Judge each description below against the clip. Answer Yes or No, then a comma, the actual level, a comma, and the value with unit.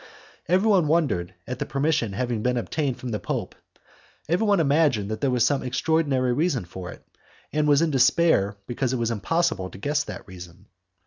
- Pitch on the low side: Yes, low, 130 Hz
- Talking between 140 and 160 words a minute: No, average, 180 wpm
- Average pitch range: No, wide, 6.4 semitones